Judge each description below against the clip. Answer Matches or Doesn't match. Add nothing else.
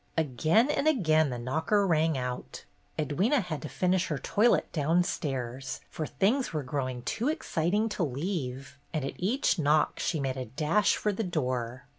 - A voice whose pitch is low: Doesn't match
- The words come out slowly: Doesn't match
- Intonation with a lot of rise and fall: Matches